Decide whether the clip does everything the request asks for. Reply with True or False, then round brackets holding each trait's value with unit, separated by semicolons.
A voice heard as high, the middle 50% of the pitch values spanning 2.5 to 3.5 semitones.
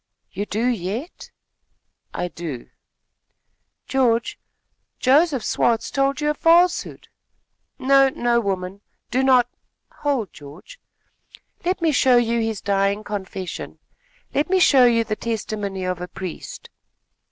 False (230 Hz; 5.5 semitones)